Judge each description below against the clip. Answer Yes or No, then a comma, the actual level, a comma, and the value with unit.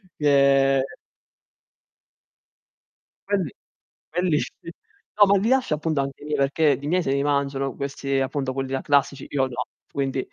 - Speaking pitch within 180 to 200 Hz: No, medium, 140 Hz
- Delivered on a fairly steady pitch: Yes, narrow, 2.0 semitones